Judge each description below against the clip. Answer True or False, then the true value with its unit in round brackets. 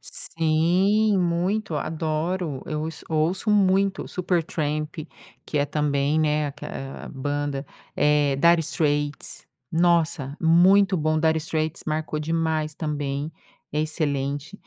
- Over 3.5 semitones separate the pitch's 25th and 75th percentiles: False (2.6 semitones)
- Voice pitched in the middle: True (155 Hz)